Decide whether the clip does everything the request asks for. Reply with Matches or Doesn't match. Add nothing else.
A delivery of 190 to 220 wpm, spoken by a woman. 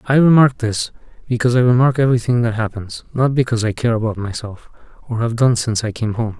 Doesn't match